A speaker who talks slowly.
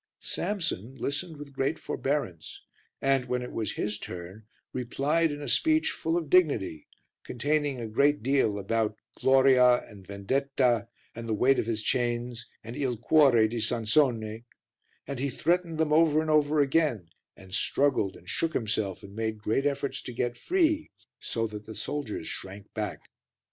No: average, 160 wpm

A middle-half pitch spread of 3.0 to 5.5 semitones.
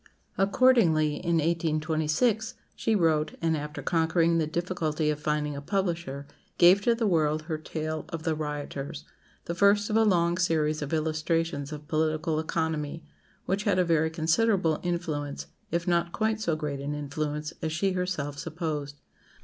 No: narrow, 2.4 semitones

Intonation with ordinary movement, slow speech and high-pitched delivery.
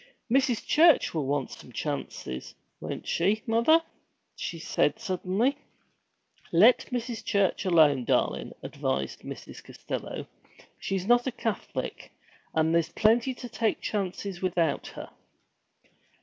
No: wide, 6.2 semitones; slow, 120 wpm; high, 200 Hz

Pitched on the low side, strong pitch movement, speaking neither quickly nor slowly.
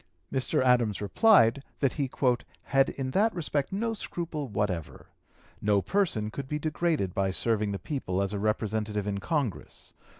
Yes: low, 125 Hz; wide, 6.6 semitones; average, 155 wpm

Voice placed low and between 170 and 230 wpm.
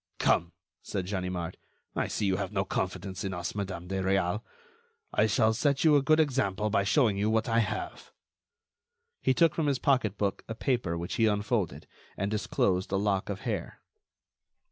Yes: low, 105 Hz; average, 175 wpm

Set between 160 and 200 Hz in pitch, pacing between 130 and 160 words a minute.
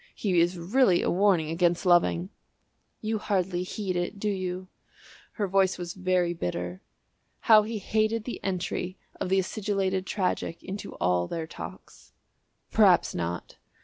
Yes: medium, 185 Hz; average, 145 wpm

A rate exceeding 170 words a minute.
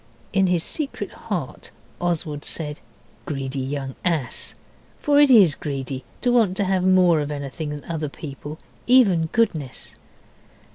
No: average, 140 wpm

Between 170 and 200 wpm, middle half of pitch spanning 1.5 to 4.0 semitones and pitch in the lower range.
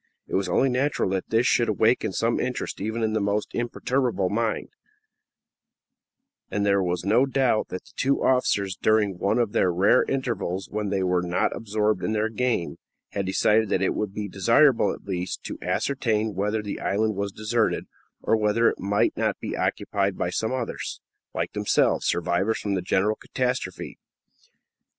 Yes: average, 175 wpm; average, 3.1 semitones; low, 105 Hz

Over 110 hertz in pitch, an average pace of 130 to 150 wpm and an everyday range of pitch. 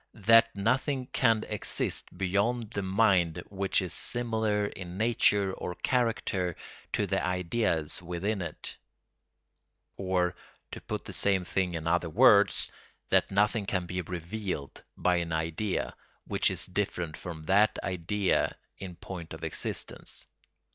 No: very low, 95 Hz; slow, 135 wpm; average, 3.4 semitones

